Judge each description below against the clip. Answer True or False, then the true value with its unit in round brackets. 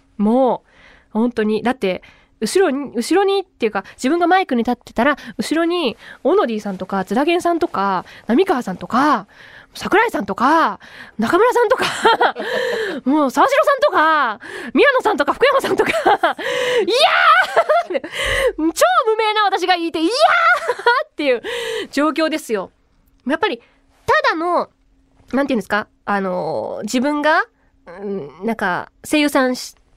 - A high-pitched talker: True (310 Hz)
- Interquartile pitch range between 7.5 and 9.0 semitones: True (8.4 semitones)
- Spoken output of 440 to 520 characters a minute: False (285 characters per minute)